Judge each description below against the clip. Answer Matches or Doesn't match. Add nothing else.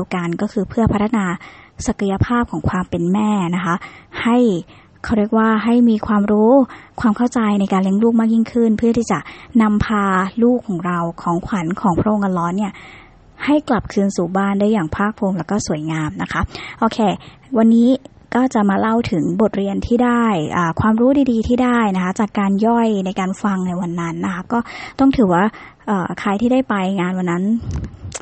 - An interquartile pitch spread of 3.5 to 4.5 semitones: Matches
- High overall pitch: Matches